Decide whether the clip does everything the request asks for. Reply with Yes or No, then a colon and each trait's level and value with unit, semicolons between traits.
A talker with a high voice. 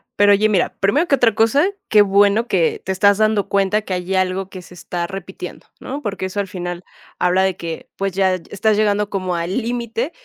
Yes: high, 195 Hz